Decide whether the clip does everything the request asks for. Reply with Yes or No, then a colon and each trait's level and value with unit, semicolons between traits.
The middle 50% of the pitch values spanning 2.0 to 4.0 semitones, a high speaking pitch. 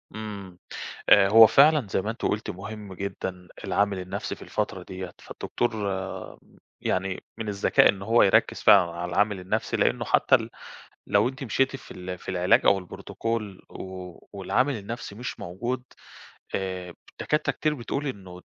No: average, 3.6 semitones; low, 100 Hz